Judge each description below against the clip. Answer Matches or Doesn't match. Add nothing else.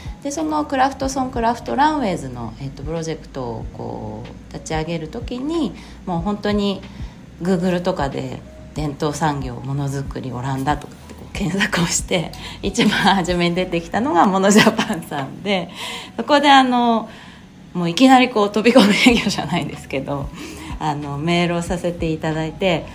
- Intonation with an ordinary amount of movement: Doesn't match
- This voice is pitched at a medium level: Matches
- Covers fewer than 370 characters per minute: Matches